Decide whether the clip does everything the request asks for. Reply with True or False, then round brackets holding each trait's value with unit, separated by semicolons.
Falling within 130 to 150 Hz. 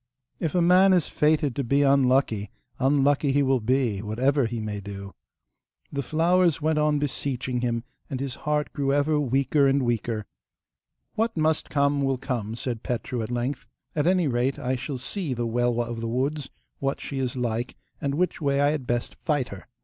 True (135 Hz)